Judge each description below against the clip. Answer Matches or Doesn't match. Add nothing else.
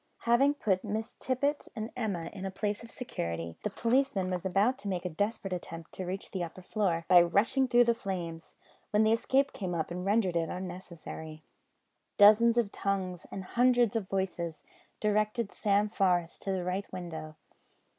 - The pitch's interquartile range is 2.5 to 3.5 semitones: Doesn't match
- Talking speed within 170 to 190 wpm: Matches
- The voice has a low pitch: Doesn't match